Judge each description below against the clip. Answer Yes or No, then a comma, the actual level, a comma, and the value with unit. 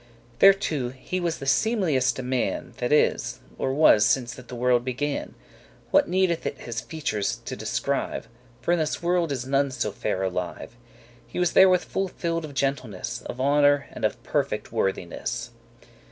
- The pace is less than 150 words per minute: No, average, 165 wpm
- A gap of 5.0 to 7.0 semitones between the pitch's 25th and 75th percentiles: Yes, wide, 5.4 semitones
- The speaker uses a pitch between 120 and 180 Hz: Yes, low, 135 Hz